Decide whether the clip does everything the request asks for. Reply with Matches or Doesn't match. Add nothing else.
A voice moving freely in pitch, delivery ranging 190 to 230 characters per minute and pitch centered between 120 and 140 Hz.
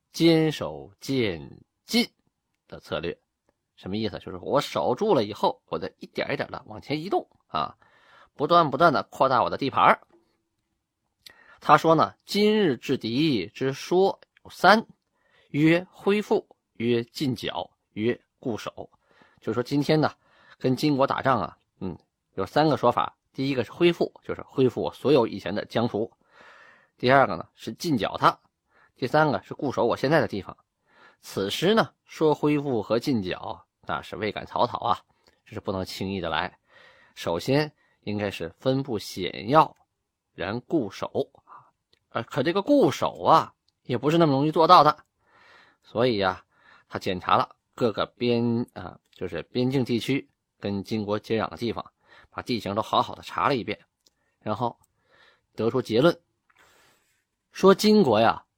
Matches